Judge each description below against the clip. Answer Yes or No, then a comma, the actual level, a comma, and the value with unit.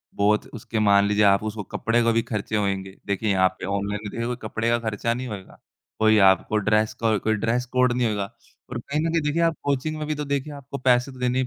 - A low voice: Yes, low, 115 Hz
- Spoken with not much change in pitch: No, average, 3.7 semitones